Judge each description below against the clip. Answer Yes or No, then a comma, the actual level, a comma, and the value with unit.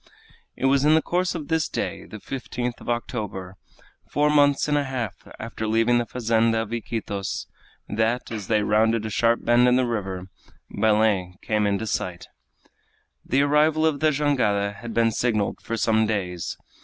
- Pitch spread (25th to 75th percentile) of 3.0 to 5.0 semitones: Yes, average, 3.9 semitones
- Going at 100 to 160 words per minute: No, average, 170 wpm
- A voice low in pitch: Yes, low, 115 Hz